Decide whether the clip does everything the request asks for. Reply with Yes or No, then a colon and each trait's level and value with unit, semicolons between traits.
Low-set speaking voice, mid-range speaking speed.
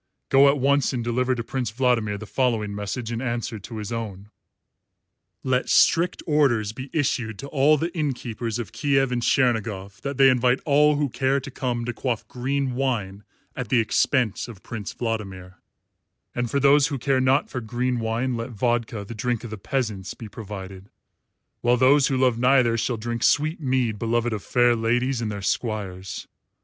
Yes: low, 120 Hz; average, 185 wpm